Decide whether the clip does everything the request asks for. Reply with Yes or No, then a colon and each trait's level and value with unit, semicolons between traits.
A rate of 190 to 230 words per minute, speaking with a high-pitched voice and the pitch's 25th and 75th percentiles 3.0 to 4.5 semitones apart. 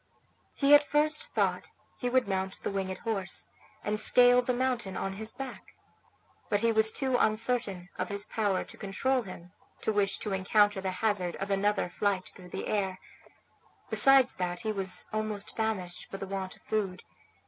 No: average, 175 wpm; high, 205 Hz; average, 3.7 semitones